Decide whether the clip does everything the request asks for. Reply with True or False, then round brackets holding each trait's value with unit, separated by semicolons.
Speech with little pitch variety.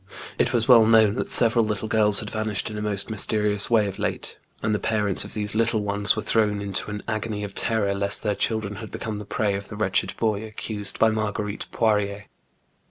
True (1.3 semitones)